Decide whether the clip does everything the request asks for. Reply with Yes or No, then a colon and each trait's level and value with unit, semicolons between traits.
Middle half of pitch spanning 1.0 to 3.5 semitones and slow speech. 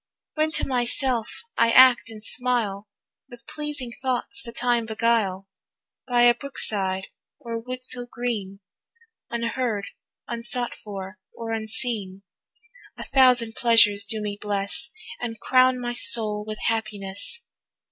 Yes: average, 2.9 semitones; slow, 125 wpm